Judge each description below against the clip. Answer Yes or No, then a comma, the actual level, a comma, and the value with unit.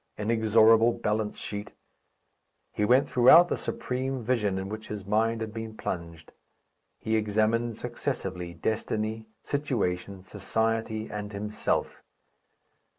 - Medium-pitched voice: No, low, 110 Hz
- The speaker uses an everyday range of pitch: No, narrow, 1.8 semitones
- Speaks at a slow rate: Yes, slow, 110 wpm